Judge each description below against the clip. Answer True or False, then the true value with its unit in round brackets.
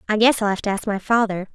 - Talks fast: True (310 wpm)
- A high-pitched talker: True (210 Hz)